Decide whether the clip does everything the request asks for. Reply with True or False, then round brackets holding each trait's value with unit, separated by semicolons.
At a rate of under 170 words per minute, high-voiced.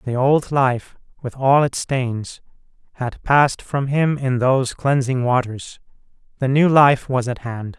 False (160 wpm; 130 Hz)